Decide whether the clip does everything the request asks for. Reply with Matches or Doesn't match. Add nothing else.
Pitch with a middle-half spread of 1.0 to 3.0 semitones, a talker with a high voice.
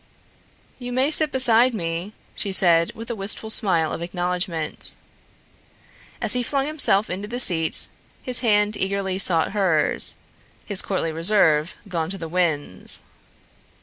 Doesn't match